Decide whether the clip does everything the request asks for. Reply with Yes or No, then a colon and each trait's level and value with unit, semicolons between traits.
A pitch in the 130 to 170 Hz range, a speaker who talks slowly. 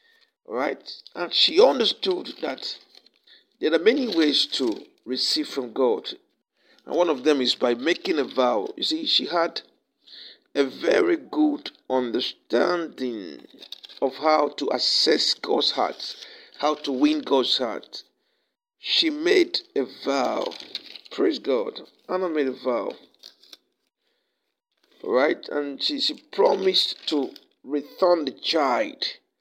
No: very high, 305 Hz; slow, 125 wpm